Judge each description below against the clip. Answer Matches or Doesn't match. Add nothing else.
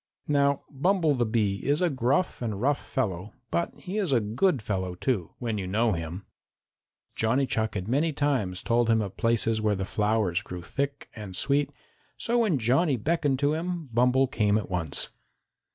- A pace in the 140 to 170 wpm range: Doesn't match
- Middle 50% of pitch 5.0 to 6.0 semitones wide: Matches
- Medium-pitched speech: Doesn't match